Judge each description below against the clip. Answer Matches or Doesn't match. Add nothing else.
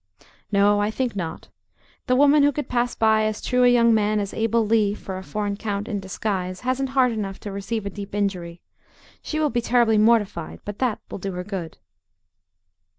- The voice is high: Matches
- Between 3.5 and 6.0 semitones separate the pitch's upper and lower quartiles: Doesn't match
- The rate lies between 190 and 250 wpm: Matches